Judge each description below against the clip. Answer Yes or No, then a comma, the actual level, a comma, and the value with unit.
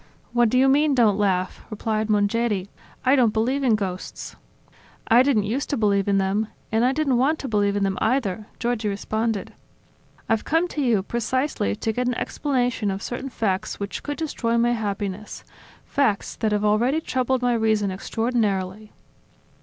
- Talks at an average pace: Yes, average, 170 wpm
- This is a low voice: No, high, 225 Hz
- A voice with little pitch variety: No, average, 3.7 semitones